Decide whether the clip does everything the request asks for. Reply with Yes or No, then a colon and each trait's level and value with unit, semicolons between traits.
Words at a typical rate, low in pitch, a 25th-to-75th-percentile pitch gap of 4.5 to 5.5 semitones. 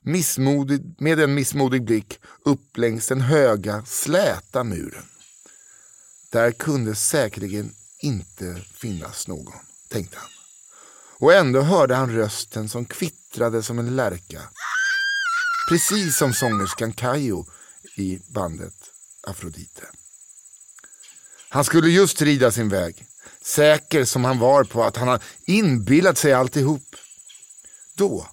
No: slow, 115 wpm; low, 130 Hz; average, 5.0 semitones